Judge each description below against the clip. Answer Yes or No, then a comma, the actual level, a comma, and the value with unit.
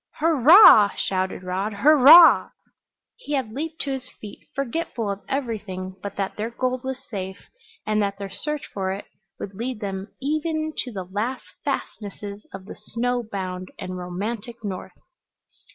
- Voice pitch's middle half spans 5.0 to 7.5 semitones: Yes, average, 5.3 semitones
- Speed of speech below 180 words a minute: Yes, average, 155 wpm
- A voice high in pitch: Yes, high, 215 Hz